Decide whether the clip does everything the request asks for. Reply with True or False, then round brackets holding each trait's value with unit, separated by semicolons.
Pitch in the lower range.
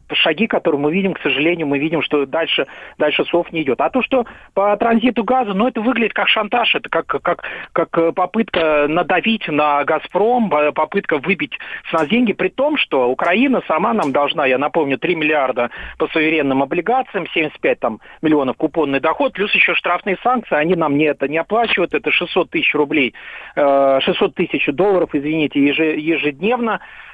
False (170 Hz)